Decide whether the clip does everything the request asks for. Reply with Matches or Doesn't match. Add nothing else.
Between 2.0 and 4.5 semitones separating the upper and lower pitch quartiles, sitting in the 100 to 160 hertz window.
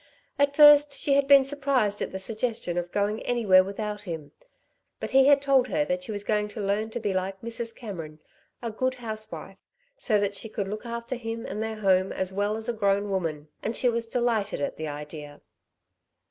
Doesn't match